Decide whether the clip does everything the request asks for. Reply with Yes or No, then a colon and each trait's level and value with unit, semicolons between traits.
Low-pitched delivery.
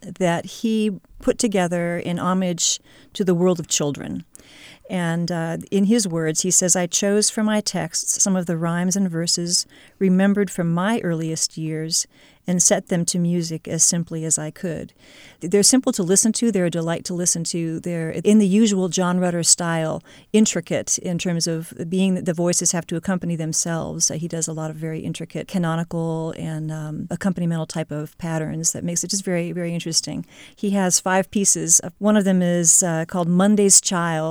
No: medium, 175 Hz